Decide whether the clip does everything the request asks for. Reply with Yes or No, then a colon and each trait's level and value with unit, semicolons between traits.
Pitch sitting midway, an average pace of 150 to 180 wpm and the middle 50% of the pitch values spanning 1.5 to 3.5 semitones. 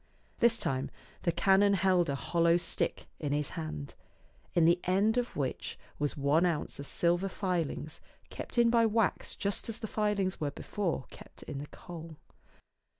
No: medium, 175 Hz; average, 165 wpm; average, 5.2 semitones